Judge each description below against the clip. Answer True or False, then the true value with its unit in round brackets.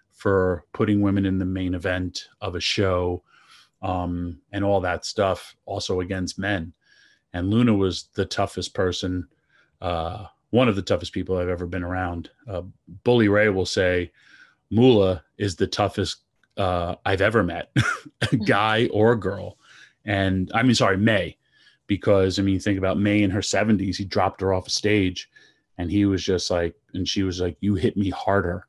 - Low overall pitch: True (95 Hz)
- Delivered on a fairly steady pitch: True (2.2 semitones)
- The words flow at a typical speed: True (180 wpm)